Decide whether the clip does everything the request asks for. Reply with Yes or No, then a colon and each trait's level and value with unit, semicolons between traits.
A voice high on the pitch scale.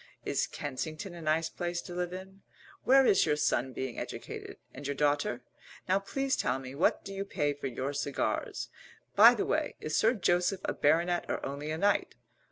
No: medium, 160 Hz